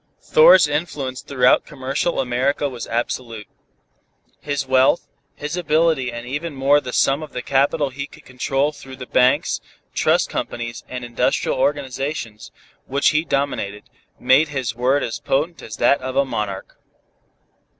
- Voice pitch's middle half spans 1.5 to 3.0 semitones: Yes, average, 2.7 semitones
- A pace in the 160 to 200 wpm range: No, average, 145 wpm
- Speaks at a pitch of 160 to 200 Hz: No, low, 135 Hz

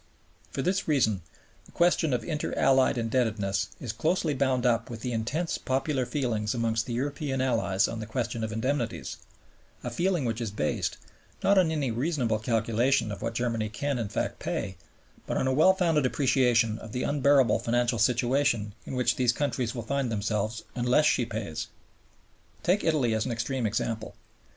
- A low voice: Yes, low, 120 Hz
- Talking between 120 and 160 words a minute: No, average, 175 wpm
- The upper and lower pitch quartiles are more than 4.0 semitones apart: No, average, 3.7 semitones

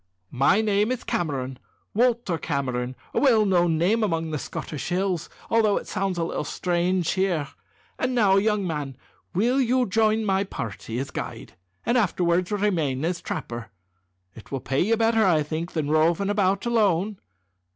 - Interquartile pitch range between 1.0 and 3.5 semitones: No, average, 5.2 semitones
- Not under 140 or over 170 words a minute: Yes, average, 160 wpm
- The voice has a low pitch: No, medium, 185 Hz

